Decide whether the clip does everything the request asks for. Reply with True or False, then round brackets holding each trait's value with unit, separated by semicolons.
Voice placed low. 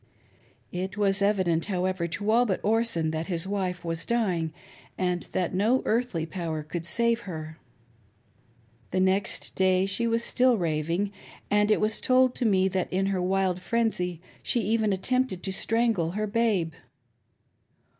False (190 Hz)